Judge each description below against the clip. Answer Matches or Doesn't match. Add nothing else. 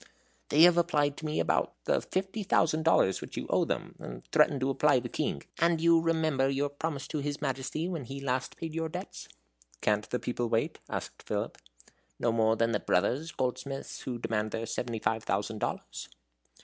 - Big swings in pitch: Matches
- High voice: Doesn't match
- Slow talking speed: Doesn't match